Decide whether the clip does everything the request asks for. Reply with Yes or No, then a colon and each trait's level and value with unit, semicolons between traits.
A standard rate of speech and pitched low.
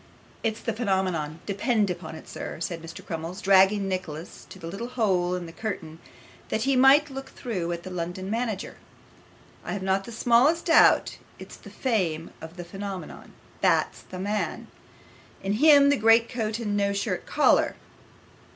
No: average, 165 wpm; high, 200 Hz